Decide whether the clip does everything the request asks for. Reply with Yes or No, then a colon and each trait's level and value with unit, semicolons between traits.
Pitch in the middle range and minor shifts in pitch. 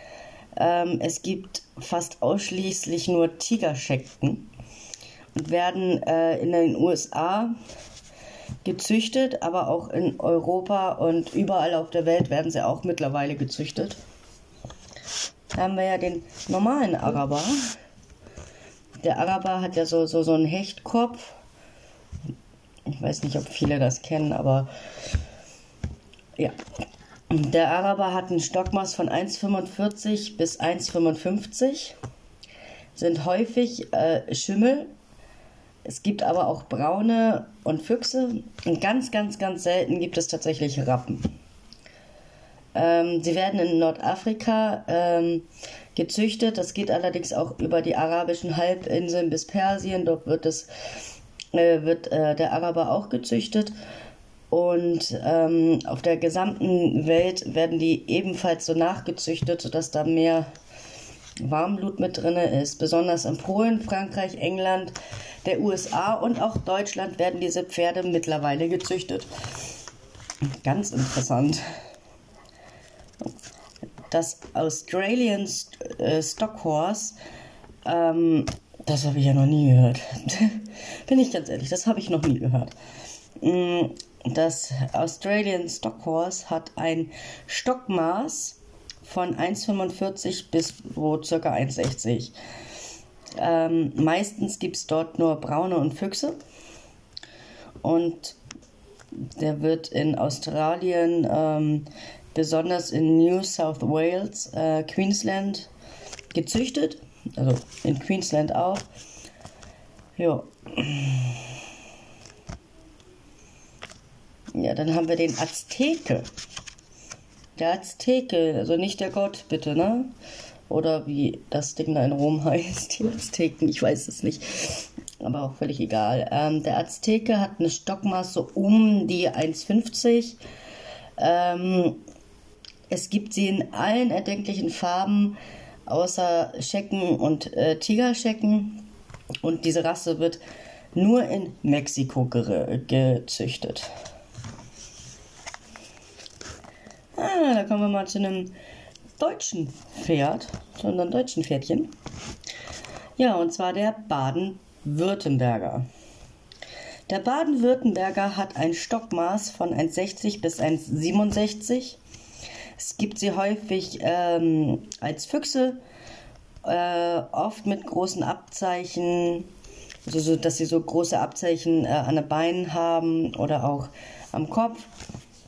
No: medium, 170 Hz; average, 3.7 semitones